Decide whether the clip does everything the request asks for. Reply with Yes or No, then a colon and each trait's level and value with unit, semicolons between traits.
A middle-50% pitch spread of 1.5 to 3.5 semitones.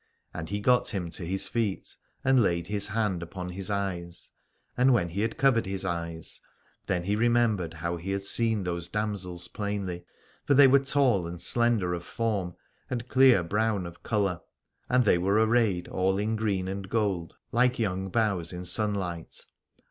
No: average, 4.2 semitones